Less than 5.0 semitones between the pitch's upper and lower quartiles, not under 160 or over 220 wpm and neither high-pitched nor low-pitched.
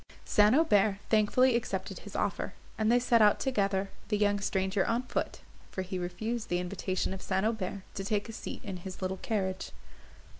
No: average, 2.7 semitones; average, 185 wpm; high, 205 Hz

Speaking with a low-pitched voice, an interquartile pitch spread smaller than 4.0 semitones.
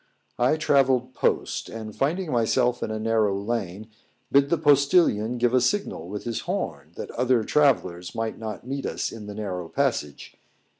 No: low, 120 Hz; average, 4.4 semitones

